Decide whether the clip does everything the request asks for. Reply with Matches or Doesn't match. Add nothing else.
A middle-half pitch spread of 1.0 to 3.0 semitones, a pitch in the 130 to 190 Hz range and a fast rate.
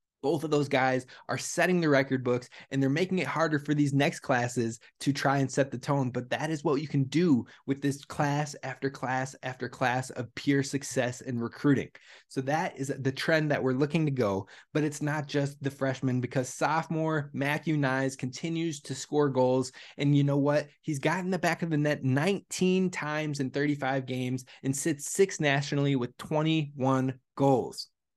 Doesn't match